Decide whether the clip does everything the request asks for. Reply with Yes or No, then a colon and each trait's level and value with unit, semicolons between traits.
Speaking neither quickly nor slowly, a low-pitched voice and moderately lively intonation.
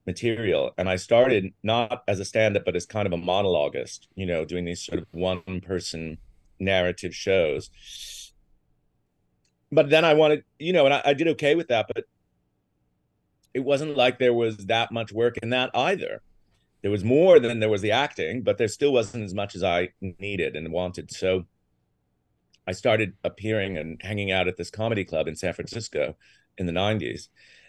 Yes: average, 185 wpm; low, 100 Hz; average, 4.8 semitones